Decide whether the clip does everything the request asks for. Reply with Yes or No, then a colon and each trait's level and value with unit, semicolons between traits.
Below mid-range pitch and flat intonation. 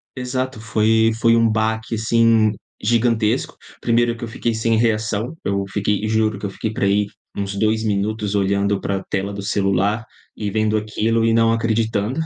Yes: low, 110 Hz; narrow, 1.9 semitones